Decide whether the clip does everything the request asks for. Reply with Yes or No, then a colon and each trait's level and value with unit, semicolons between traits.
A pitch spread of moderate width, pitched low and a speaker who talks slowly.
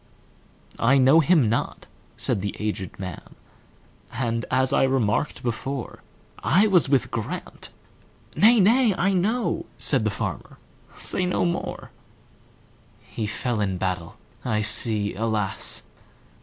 No: wide, 8.2 semitones; low, 120 Hz; slow, 100 wpm